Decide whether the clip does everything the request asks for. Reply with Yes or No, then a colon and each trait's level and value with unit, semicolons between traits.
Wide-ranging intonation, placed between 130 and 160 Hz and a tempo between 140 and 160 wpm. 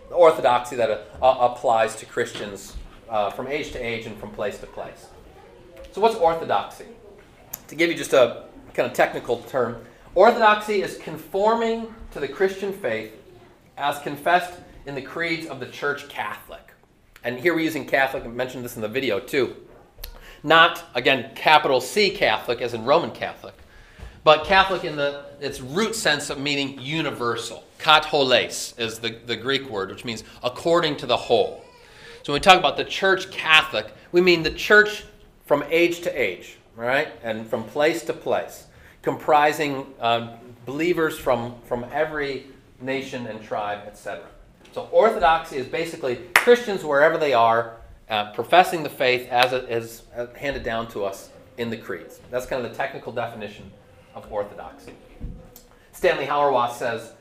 Yes: wide, 6.1 semitones; low, 135 Hz; average, 155 wpm